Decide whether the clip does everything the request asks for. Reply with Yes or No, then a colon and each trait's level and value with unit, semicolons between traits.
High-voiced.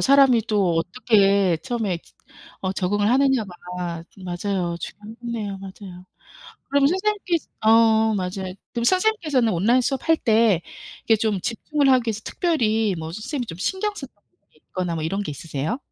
Yes: high, 220 Hz